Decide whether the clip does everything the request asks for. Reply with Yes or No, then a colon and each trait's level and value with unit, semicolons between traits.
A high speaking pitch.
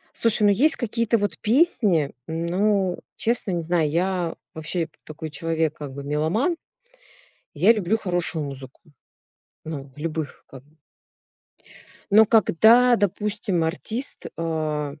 No: medium, 175 Hz